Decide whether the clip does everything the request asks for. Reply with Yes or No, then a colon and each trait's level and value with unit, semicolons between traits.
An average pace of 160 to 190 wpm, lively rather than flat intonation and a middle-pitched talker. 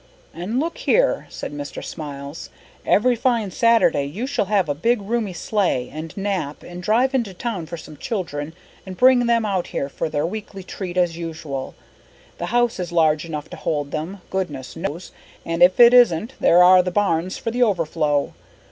Yes: average, 185 wpm; wide, 5.9 semitones; medium, 180 Hz